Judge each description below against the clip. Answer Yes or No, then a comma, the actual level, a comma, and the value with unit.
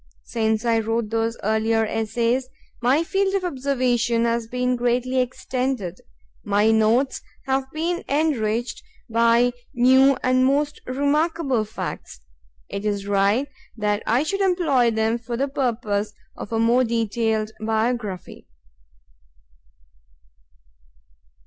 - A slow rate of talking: Yes, slow, 115 wpm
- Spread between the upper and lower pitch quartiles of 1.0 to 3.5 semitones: Yes, average, 3.2 semitones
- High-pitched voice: Yes, high, 235 Hz